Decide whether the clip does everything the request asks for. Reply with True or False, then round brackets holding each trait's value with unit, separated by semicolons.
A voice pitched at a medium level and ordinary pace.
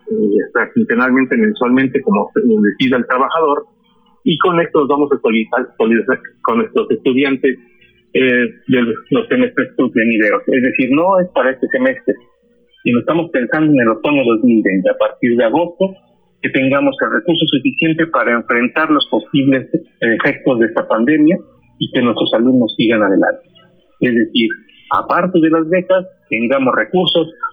True (170 Hz; 150 wpm)